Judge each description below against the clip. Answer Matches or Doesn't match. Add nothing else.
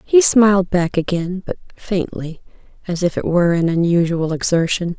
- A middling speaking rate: Matches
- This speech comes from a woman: Matches